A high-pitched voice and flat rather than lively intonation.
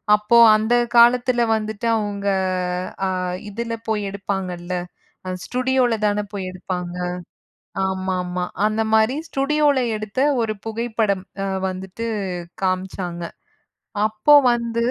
No: high, 215 Hz; average, 3.7 semitones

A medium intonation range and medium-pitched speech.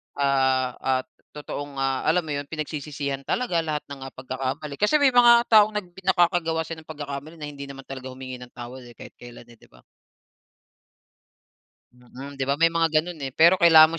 Yes: average, 3.7 semitones; medium, 145 Hz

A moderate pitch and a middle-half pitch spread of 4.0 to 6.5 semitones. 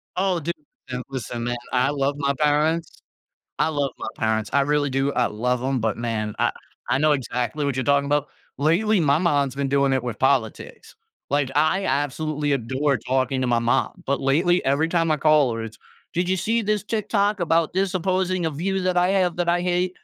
Yes: medium, 145 Hz; average, 4.9 semitones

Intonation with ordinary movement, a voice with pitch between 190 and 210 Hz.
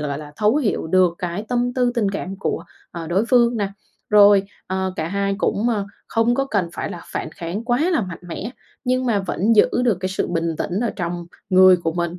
Yes: average, 4.7 semitones; high, 195 Hz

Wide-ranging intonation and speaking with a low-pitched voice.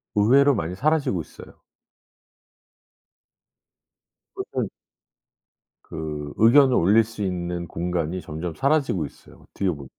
Yes: wide, 6.5 semitones; very low, 90 Hz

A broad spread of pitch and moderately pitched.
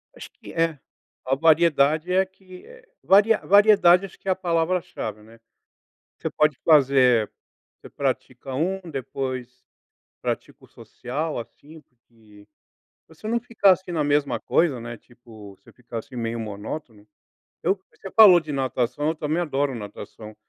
Yes: wide, 6.6 semitones; medium, 145 Hz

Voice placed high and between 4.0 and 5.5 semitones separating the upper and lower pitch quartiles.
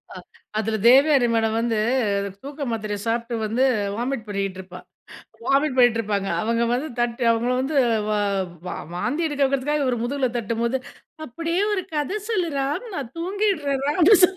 Yes: very high, 255 Hz; average, 4.6 semitones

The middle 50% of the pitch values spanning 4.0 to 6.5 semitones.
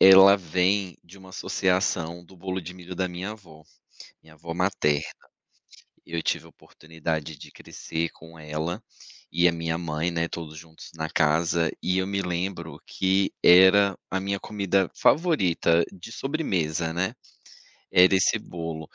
No: narrow, 2.6 semitones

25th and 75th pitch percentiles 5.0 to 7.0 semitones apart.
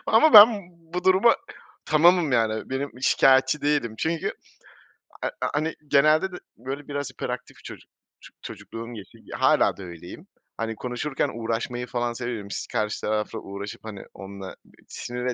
Yes: wide, 5.5 semitones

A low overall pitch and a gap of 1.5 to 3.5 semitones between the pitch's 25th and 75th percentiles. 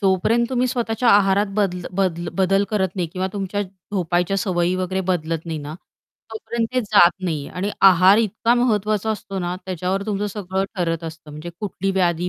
No: high, 190 Hz; average, 2.9 semitones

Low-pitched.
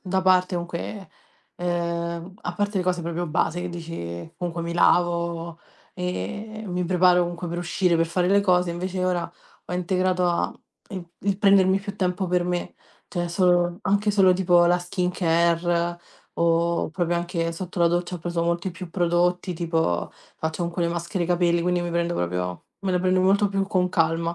No: medium, 175 Hz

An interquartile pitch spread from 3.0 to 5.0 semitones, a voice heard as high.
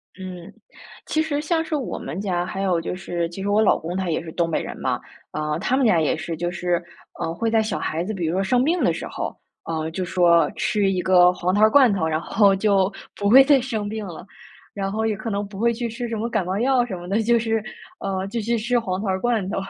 Yes: average, 4.4 semitones; high, 195 Hz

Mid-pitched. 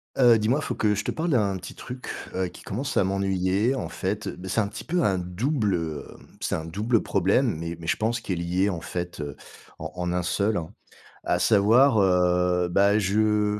No: low, 100 Hz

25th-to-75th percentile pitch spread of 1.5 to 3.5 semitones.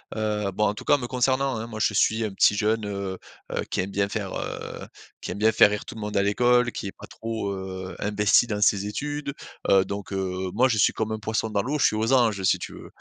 Yes: narrow, 2.4 semitones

